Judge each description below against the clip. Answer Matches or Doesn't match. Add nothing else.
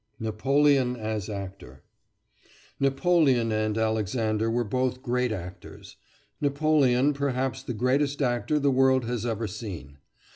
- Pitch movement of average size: Matches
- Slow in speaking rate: Matches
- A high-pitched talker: Doesn't match